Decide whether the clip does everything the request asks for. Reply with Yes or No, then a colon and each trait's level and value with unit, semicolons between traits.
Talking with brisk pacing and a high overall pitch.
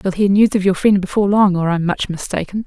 Yes: fast, 270 wpm; high, 195 Hz